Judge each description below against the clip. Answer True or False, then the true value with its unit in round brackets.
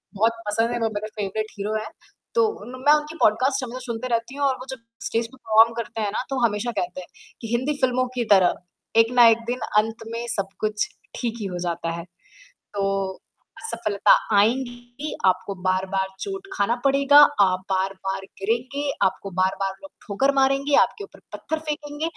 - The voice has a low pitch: False (230 Hz)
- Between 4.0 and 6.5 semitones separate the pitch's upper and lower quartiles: True (4.6 semitones)